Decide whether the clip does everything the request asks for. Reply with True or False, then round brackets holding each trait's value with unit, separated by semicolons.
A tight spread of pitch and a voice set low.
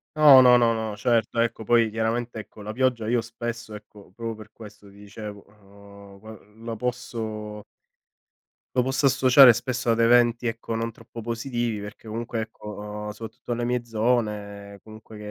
True (2.1 semitones; 115 Hz)